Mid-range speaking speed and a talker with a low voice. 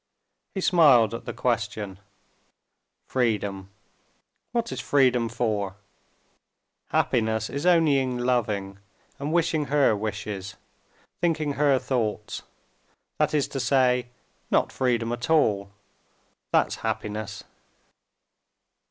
No: slow, 100 wpm; low, 120 Hz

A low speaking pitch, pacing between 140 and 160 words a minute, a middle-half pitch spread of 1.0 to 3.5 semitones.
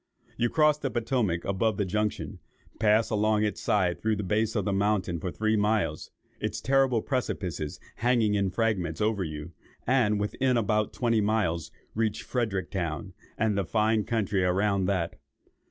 Yes: low, 105 Hz; average, 155 wpm; average, 2.9 semitones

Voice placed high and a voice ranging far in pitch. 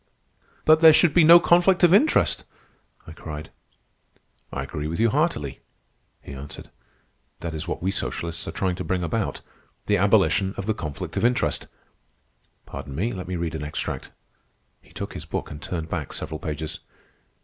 No: very low, 90 Hz; wide, 7.1 semitones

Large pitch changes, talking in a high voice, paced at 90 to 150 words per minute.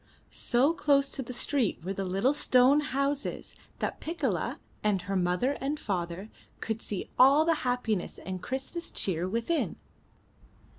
Yes: wide, 6.4 semitones; very high, 250 Hz; average, 145 wpm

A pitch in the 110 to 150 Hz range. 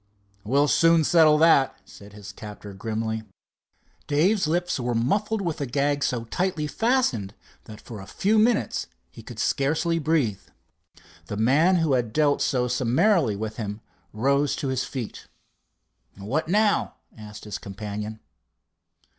Yes: low, 135 Hz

